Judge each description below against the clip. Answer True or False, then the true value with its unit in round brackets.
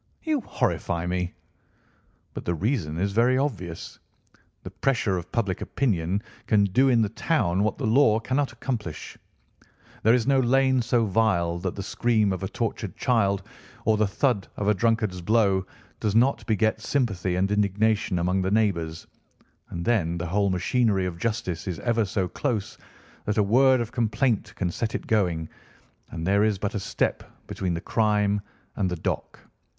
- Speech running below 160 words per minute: False (170 wpm)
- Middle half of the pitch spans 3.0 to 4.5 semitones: True (4.0 semitones)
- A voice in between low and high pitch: False (105 Hz)